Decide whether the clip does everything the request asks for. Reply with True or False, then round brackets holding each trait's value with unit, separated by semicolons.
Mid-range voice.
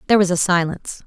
True (180 Hz)